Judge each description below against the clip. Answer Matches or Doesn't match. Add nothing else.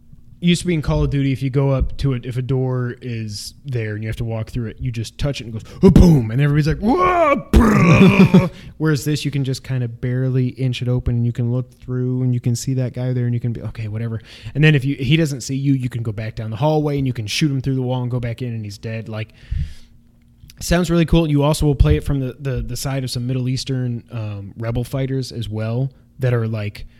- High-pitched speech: Doesn't match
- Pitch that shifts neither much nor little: Matches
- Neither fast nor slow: Doesn't match